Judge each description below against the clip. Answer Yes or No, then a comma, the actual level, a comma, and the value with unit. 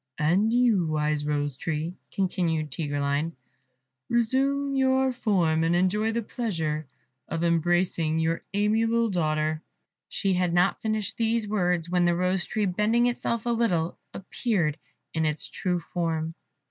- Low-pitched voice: No, medium, 180 Hz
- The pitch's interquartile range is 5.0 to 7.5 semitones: Yes, wide, 5.6 semitones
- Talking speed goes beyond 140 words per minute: No, slow, 135 wpm